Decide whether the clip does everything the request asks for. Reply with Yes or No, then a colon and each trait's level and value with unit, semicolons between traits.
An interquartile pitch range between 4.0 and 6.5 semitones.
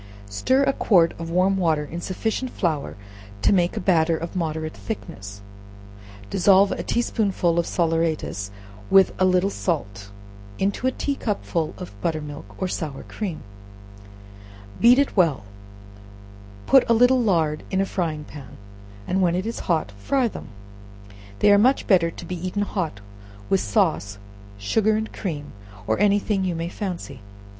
Yes: average, 4.4 semitones